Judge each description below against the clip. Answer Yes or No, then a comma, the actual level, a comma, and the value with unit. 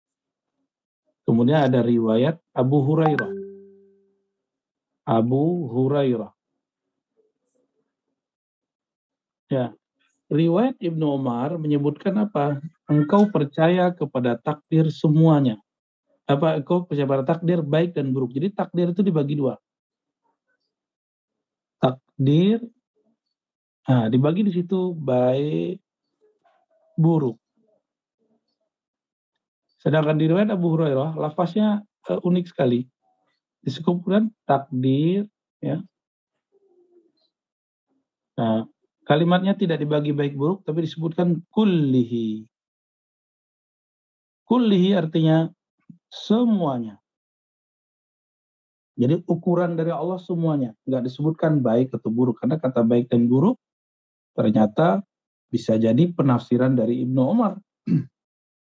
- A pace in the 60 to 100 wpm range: Yes, slow, 85 wpm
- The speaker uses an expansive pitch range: Yes, wide, 6.9 semitones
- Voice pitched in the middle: Yes, medium, 160 Hz